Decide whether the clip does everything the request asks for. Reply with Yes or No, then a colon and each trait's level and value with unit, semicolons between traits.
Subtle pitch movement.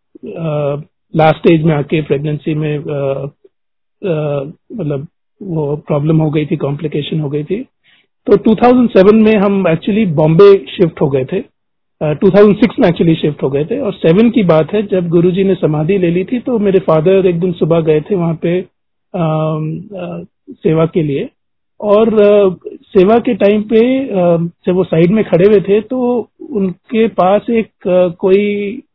No: average, 4.6 semitones